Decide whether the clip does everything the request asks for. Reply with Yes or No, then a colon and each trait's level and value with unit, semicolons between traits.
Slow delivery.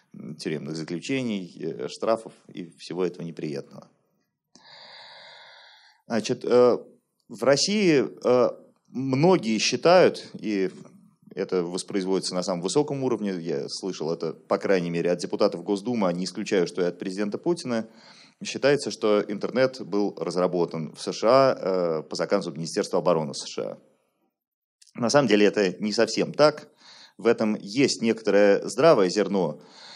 No: average, 125 wpm